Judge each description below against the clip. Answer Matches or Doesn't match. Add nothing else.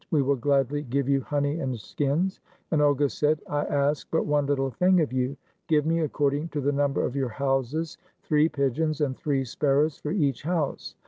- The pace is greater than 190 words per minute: Matches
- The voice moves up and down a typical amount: Doesn't match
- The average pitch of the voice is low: Doesn't match